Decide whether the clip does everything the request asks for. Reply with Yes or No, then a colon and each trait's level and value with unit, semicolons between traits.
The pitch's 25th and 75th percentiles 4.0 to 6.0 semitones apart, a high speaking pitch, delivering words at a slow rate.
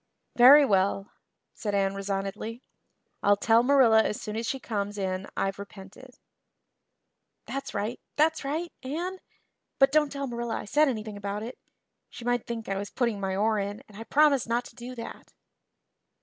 No: average, 4.7 semitones; high, 225 Hz; average, 170 wpm